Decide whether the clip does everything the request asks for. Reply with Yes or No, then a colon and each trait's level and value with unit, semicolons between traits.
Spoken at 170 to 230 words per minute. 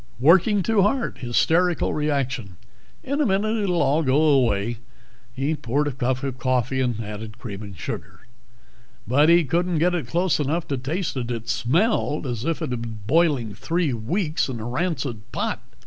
Yes: average, 175 wpm